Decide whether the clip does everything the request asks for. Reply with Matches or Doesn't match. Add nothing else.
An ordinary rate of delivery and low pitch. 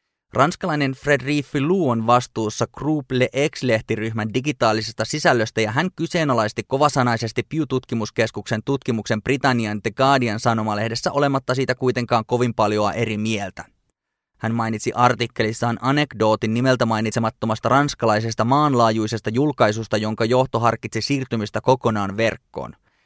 Matches